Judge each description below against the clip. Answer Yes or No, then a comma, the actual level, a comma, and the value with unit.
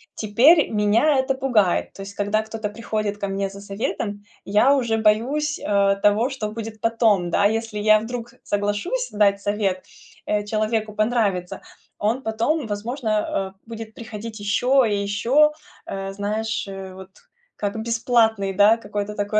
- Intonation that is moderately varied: No, narrow, 2.2 semitones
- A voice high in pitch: Yes, high, 215 Hz